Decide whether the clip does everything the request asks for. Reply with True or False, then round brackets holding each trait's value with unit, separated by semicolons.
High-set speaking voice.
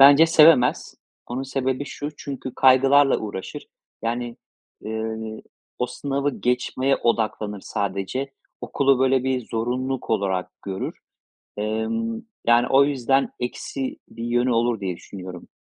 False (125 Hz)